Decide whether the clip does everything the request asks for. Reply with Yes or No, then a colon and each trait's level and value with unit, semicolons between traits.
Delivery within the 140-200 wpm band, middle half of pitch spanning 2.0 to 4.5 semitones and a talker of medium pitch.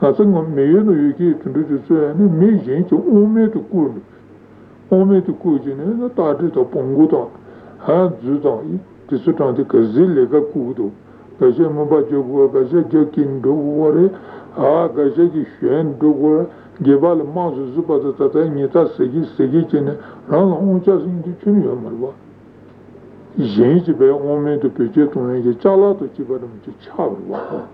No: average, 145 wpm; average, 5.1 semitones; medium, 160 Hz